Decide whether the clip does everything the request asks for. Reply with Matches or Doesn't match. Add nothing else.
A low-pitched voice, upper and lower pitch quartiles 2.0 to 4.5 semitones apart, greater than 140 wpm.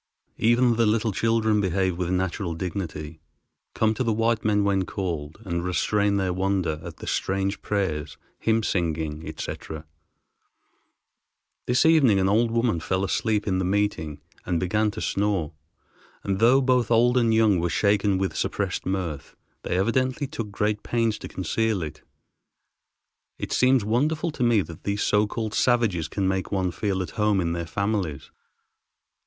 Matches